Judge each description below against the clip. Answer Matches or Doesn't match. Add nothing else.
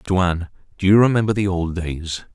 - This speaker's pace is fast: Doesn't match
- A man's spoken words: Matches